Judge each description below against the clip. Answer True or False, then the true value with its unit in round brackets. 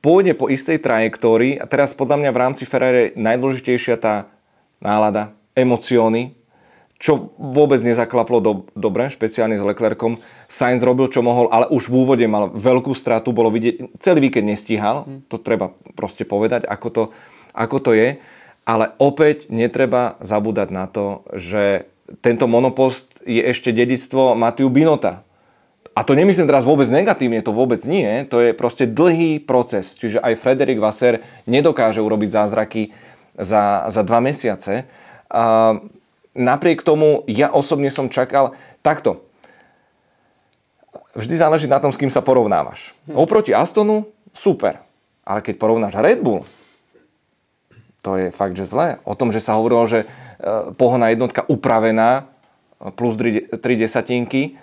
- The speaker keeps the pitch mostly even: False (3.2 semitones)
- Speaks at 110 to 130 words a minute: False (140 wpm)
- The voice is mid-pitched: False (120 Hz)